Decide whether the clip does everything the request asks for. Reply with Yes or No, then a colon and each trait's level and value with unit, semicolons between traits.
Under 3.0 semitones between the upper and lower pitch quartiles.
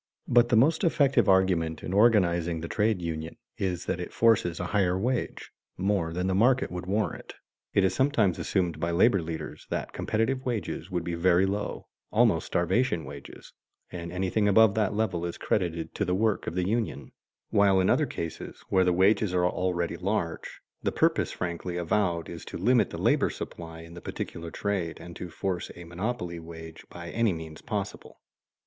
No: average, 3.6 semitones